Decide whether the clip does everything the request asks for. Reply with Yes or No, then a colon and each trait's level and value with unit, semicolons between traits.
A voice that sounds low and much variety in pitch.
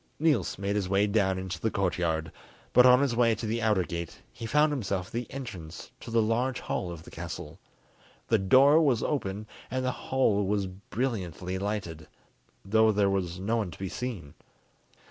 No: low, 105 Hz; average, 4.4 semitones